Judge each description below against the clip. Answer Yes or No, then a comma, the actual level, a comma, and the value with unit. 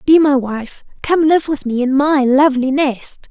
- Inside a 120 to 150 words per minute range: No, average, 200 wpm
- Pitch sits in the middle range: No, very high, 275 Hz